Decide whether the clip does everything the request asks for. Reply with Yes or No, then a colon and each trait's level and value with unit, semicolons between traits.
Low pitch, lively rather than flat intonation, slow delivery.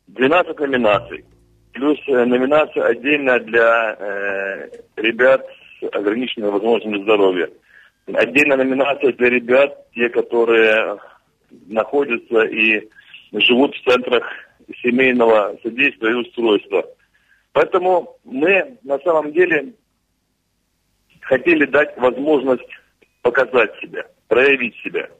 Yes: low, 130 Hz; wide, 8.0 semitones; slow, 95 wpm